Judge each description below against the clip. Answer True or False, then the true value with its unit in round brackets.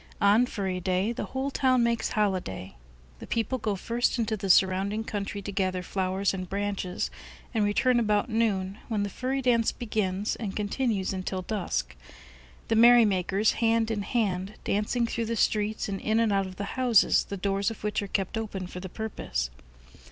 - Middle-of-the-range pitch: False (205 Hz)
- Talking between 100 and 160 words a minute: False (180 wpm)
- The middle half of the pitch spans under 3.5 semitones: True (3.1 semitones)